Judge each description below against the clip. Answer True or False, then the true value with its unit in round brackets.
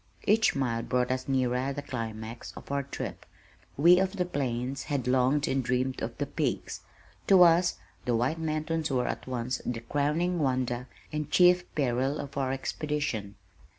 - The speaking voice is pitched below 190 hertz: True (135 Hz)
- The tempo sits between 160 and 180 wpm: True (165 wpm)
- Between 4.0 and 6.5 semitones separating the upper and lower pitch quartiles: False (3.5 semitones)